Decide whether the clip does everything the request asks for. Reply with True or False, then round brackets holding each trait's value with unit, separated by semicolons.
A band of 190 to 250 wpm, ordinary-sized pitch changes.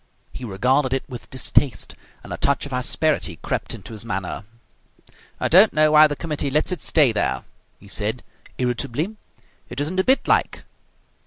False (170 wpm; 4.4 semitones)